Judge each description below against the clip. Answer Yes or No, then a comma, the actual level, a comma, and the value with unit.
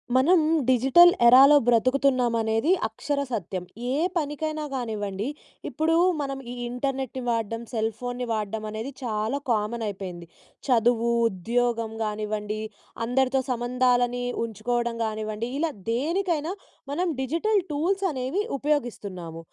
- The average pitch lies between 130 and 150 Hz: No, high, 245 Hz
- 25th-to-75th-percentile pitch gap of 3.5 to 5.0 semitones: Yes, average, 4.1 semitones